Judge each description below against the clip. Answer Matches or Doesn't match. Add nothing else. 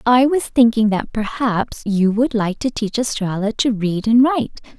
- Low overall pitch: Doesn't match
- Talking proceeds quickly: Doesn't match